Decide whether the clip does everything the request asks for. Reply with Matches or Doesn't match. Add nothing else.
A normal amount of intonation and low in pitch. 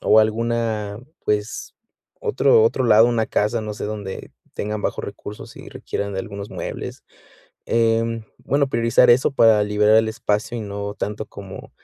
Doesn't match